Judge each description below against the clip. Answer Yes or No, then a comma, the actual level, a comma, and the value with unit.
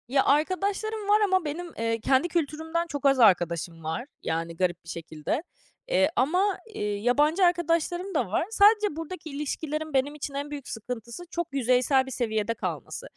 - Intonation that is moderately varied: No, wide, 7.1 semitones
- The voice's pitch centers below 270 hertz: No, very high, 290 Hz